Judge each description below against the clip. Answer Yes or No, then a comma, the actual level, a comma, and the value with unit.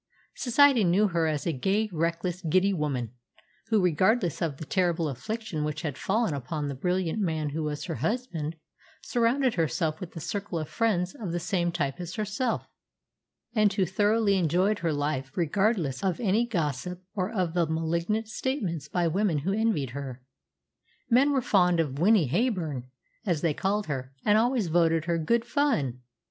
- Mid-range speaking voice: Yes, medium, 175 Hz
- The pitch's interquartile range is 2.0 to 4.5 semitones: No, wide, 5.4 semitones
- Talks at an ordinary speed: Yes, average, 170 wpm